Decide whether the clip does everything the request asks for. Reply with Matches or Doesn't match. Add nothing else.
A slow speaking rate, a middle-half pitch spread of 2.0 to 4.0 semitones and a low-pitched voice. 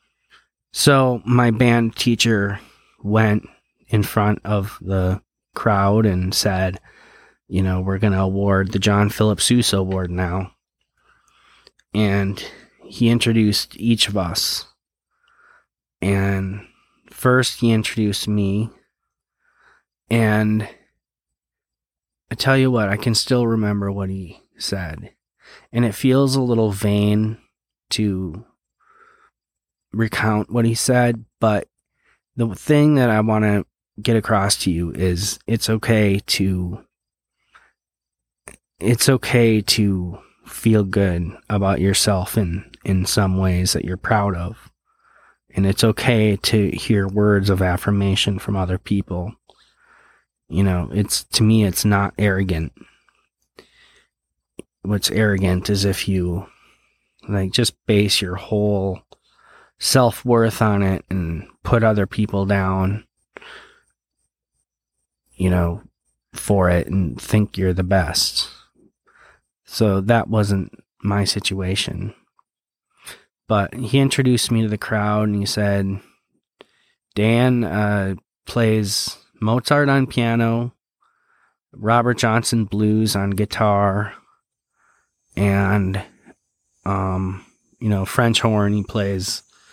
Matches